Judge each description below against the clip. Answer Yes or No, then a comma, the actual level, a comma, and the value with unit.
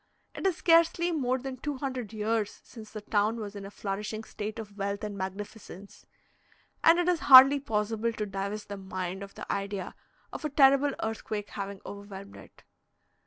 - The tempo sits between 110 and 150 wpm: No, average, 175 wpm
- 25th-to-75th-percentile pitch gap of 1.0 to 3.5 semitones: No, average, 4.6 semitones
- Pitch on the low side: No, high, 215 Hz